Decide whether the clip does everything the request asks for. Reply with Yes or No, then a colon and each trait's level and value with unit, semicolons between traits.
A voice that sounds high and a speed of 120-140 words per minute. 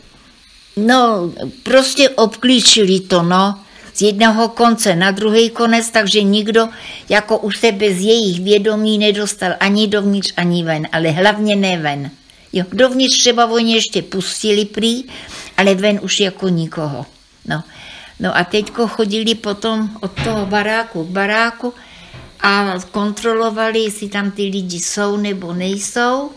Yes: high, 210 Hz; average, 135 wpm